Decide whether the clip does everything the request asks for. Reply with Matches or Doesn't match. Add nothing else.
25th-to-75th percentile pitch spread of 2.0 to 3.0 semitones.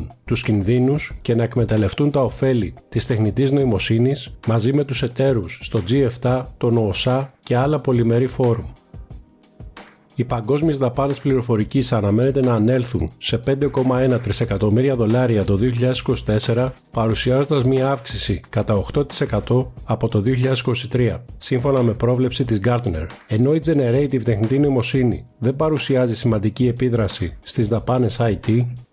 Matches